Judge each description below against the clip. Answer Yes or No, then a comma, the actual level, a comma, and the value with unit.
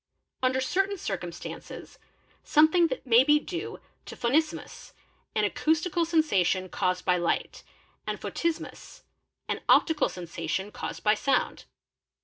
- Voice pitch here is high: Yes, very high, 265 Hz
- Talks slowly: Yes, slow, 120 wpm